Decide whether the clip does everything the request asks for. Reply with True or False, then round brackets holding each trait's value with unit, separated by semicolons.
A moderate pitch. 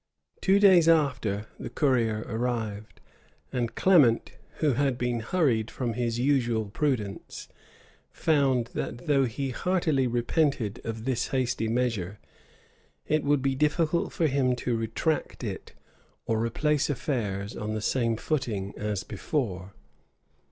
False (125 Hz)